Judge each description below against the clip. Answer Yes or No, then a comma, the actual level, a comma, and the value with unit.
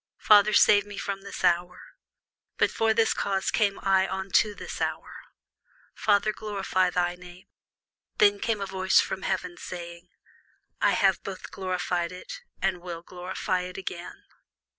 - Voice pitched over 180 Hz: Yes, high, 190 Hz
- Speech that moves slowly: No, average, 150 wpm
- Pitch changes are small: Yes, narrow, 2.1 semitones